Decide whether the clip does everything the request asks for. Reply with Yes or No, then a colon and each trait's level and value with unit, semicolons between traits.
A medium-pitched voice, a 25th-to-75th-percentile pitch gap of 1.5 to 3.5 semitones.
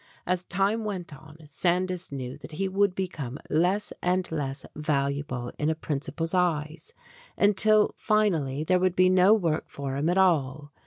No: medium, 170 Hz; average, 4.4 semitones